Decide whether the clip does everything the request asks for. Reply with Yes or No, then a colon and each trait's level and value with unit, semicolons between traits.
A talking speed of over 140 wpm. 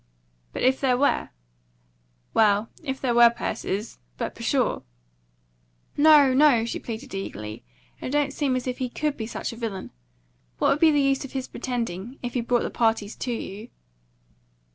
Yes: average, 170 wpm